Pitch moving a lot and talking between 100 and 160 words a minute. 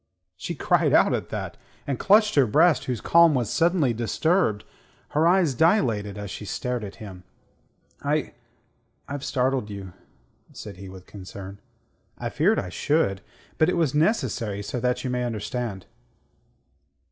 Yes: wide, 6.9 semitones; average, 150 wpm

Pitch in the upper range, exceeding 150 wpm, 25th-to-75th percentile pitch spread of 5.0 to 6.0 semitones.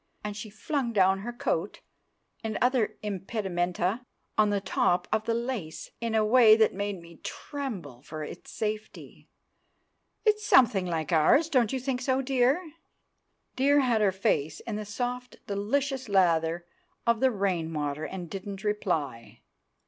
No: high, 210 Hz; average, 145 wpm; wide, 5.6 semitones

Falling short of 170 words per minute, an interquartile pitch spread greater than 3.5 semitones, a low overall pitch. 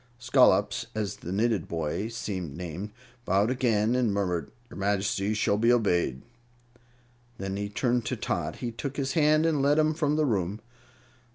Yes: average, 160 wpm; average, 4.8 semitones; low, 105 Hz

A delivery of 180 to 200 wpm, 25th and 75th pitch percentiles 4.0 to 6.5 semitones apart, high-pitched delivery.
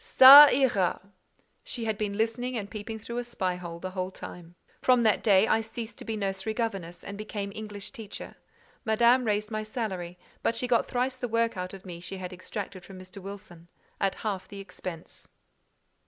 No: average, 190 wpm; average, 3.5 semitones; high, 210 Hz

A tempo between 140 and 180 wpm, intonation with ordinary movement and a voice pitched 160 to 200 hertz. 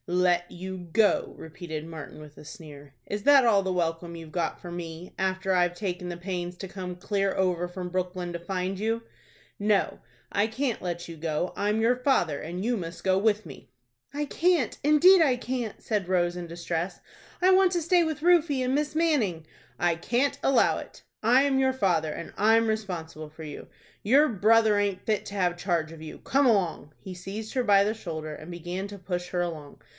No: average, 200 wpm; average, 4.7 semitones; high, 190 Hz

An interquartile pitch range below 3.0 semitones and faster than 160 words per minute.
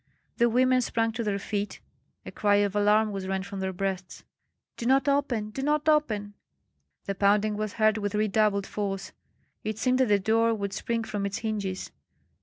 Yes: narrow, 2.4 semitones; average, 185 wpm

